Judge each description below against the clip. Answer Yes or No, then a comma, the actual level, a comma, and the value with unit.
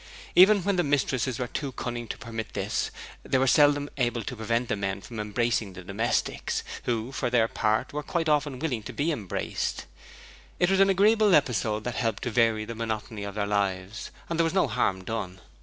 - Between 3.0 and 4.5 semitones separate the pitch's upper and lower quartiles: No, average, 5.1 semitones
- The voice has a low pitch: Yes, low, 120 Hz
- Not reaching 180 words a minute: No, fast, 205 wpm